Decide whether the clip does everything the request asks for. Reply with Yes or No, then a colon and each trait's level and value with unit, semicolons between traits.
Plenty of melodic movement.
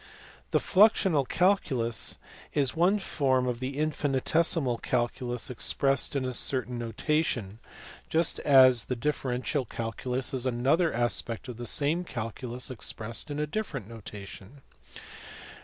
No: average, 3.9 semitones